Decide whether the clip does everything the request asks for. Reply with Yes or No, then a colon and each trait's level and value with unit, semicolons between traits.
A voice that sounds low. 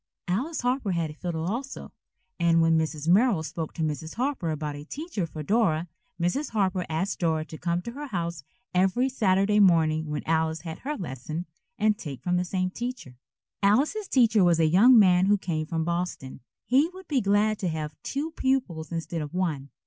No: medium, 180 Hz